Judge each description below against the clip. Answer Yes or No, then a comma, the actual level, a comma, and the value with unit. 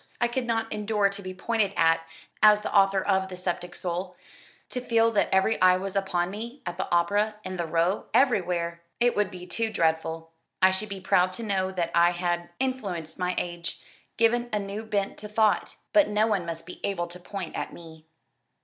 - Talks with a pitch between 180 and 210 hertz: Yes, high, 190 Hz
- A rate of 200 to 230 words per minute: Yes, fast, 205 wpm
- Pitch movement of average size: Yes, average, 3.4 semitones